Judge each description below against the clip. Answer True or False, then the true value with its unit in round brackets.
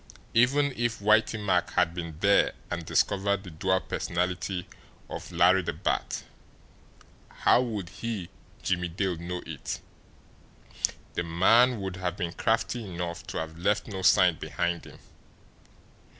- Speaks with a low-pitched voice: True (95 Hz)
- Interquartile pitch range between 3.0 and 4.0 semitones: True (3.4 semitones)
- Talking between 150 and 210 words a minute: False (135 wpm)